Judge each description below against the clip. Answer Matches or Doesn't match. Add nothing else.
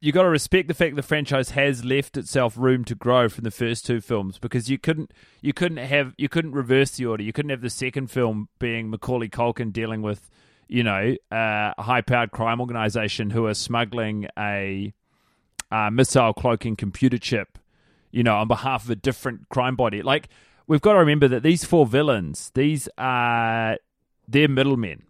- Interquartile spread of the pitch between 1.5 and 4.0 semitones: Matches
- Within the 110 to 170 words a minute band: Doesn't match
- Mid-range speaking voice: Doesn't match